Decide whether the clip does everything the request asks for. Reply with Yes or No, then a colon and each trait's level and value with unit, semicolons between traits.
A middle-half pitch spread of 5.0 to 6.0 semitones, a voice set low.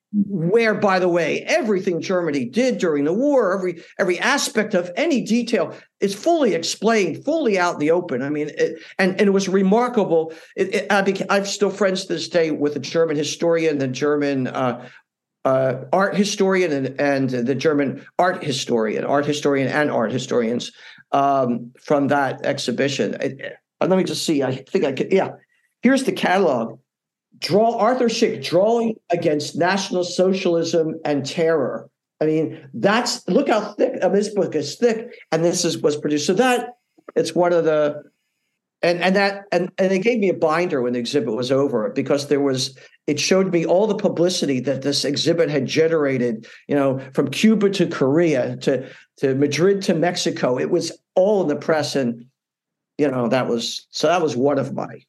No: average, 5.3 semitones; medium, 170 Hz